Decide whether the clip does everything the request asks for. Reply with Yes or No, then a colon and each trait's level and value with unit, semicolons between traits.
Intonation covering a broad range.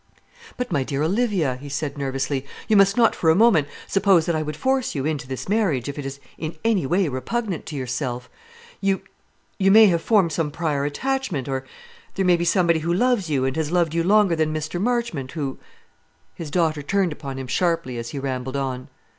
Yes: wide, 5.8 semitones